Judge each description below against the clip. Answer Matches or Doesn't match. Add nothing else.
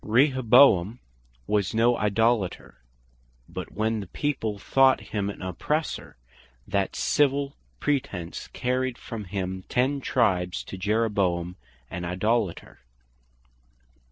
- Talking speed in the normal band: Doesn't match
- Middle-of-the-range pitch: Doesn't match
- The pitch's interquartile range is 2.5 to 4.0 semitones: Doesn't match